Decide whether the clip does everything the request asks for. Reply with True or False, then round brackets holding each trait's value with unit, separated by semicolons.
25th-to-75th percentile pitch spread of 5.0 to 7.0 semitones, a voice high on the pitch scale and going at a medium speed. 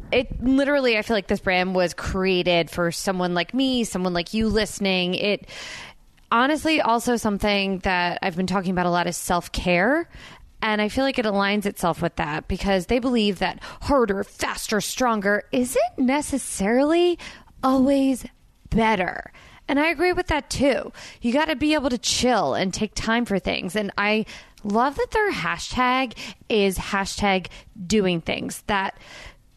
True (5.6 semitones; 215 Hz; 160 wpm)